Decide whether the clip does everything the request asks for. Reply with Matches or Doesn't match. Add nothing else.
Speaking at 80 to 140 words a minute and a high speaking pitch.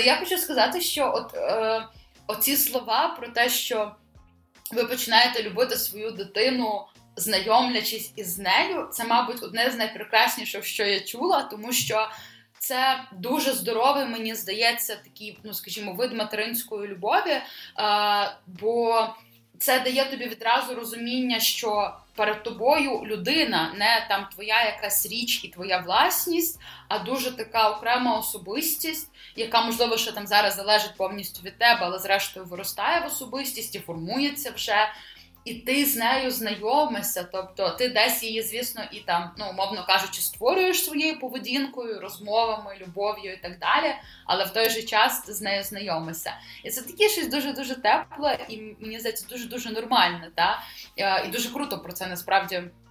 Doesn't match